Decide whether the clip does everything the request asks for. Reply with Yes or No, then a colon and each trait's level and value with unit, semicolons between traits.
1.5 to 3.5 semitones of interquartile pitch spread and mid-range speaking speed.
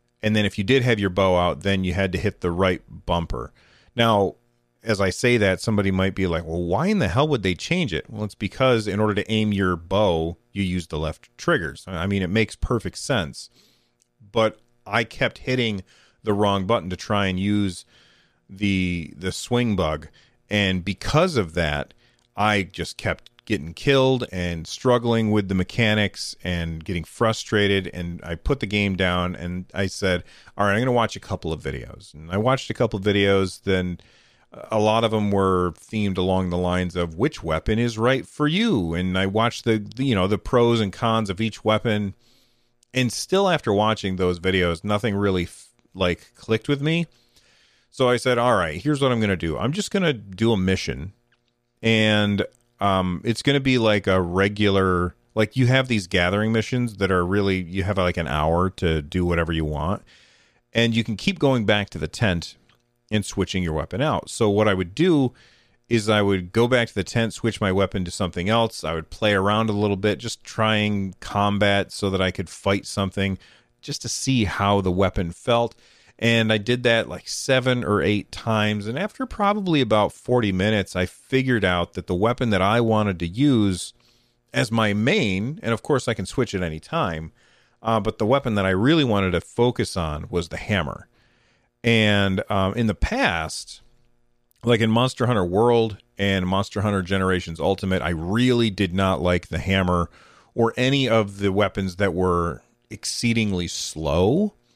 No: average, 4.2 semitones; average, 195 wpm